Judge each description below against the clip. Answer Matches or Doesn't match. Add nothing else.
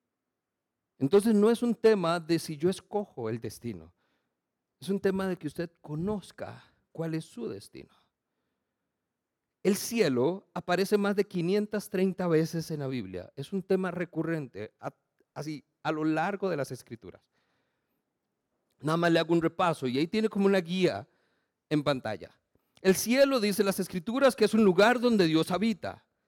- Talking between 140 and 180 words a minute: Matches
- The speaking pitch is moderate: Matches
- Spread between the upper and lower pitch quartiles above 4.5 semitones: Matches